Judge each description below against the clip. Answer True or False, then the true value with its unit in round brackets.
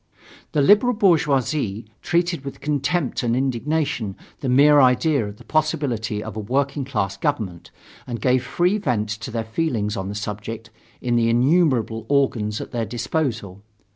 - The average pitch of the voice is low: True (125 Hz)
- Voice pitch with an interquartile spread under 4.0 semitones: False (5.1 semitones)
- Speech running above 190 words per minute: False (155 wpm)